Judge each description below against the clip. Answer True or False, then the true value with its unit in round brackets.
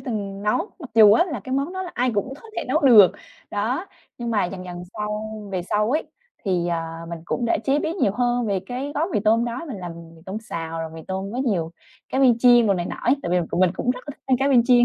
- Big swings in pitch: False (5.0 semitones)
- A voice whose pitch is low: False (225 Hz)